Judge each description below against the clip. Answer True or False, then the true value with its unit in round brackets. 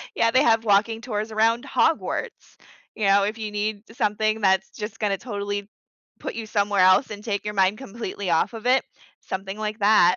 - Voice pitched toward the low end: False (210 Hz)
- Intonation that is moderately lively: False (1.9 semitones)